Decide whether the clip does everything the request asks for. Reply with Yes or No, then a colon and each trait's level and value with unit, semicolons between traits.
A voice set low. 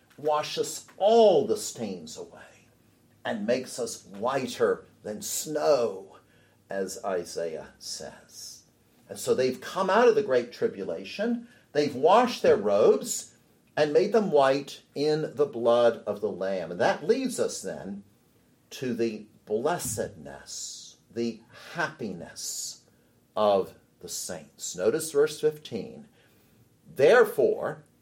No: high, 235 Hz